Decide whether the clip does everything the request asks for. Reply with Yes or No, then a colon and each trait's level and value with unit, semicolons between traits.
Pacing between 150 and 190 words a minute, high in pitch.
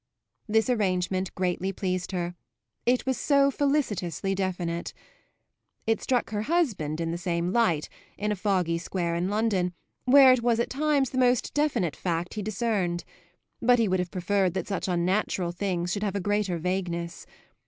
Yes: average, 165 wpm; high, 195 Hz